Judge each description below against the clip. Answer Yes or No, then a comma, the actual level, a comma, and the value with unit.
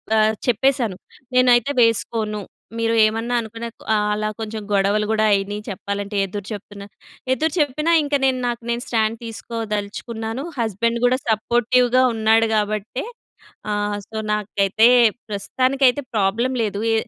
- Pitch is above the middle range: Yes, high, 220 Hz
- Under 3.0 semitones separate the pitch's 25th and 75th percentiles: Yes, narrow, 2.5 semitones